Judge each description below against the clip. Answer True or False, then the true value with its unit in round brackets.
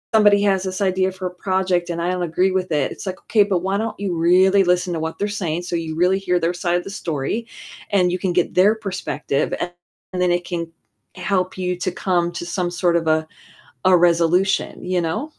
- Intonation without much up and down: True (1.7 semitones)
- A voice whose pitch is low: False (180 Hz)